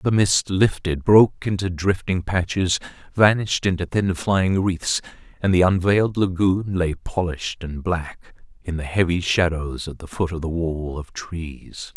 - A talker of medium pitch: No, very low, 90 Hz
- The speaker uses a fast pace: No, average, 160 wpm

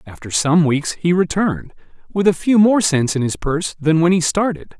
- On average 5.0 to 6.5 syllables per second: Yes, 5.1 syllables/s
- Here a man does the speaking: Yes, male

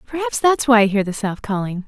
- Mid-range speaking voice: No, high, 230 Hz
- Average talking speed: No, fast, 290 wpm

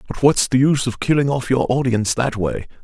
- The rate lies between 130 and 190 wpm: No, fast, 235 wpm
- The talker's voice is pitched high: No, low, 125 Hz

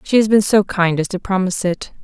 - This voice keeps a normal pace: No, fast, 265 wpm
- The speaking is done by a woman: Yes, female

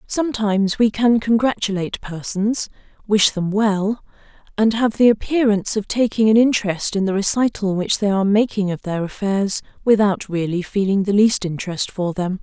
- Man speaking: No, female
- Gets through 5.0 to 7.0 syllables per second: Yes, 5.2 syllables/s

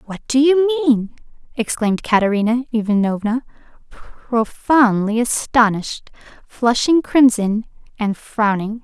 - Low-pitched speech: No, high, 235 Hz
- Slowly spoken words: Yes, slow, 90 wpm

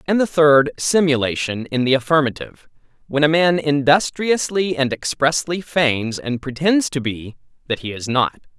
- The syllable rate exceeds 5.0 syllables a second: No, 4.7 syllables/s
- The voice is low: No, medium, 145 Hz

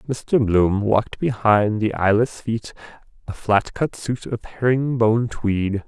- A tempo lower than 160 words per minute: Yes, slow, 135 wpm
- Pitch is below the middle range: Yes, low, 110 Hz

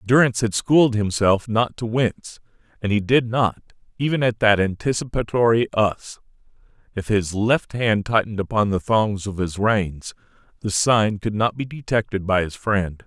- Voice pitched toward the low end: Yes, low, 110 Hz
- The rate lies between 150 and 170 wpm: Yes, average, 165 wpm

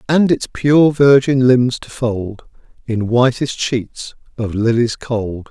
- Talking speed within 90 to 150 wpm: Yes, average, 140 wpm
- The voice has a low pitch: Yes, low, 125 Hz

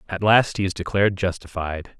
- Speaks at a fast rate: No, average, 180 wpm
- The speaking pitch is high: No, very low, 95 Hz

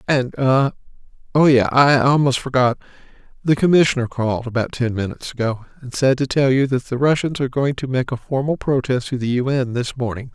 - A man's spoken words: No, female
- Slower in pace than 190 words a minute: No, average, 195 wpm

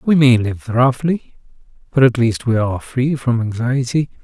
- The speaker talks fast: No, average, 170 wpm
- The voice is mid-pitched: No, low, 125 Hz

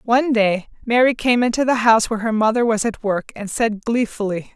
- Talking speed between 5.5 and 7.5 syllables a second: Yes, 5.6 syllables/s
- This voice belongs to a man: No, female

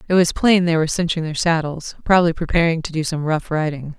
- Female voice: Yes, female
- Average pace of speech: No, fast, 225 wpm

